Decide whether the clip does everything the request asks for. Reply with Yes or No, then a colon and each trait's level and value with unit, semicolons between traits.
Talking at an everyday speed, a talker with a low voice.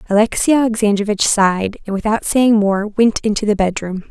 No: average, 160 wpm; high, 210 Hz